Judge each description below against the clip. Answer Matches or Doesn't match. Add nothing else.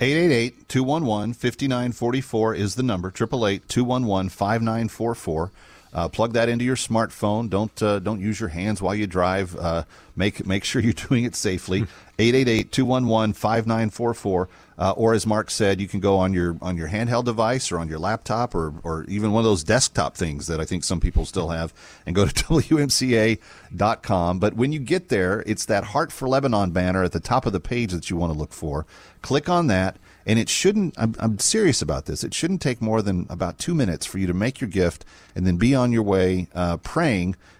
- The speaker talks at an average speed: Matches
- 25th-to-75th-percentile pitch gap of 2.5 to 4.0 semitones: Doesn't match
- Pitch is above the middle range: Doesn't match